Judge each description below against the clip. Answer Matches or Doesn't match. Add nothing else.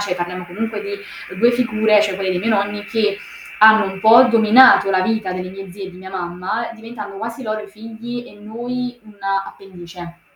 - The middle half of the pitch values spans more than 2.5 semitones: Matches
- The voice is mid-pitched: Doesn't match